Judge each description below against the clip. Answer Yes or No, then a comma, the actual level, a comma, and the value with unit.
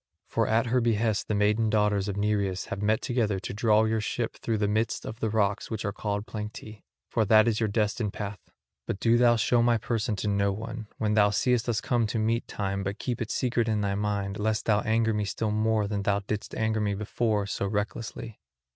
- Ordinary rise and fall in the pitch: No, narrow, 1.6 semitones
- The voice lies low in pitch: Yes, low, 110 Hz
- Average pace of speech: No, fast, 225 wpm